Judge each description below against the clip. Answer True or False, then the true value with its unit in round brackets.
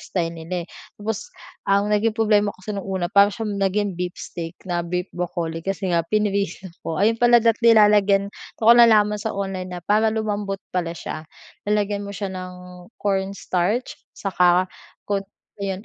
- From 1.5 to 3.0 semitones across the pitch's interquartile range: True (2.5 semitones)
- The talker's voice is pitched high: True (195 Hz)